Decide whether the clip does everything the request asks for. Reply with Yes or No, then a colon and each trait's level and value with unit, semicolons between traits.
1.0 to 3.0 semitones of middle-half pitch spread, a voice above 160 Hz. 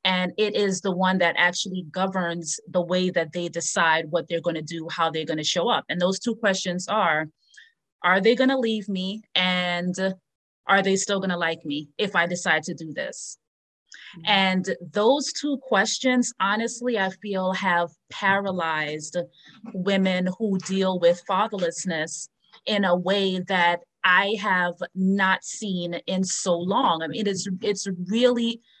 Yes: average, 2.7 semitones; medium, 185 Hz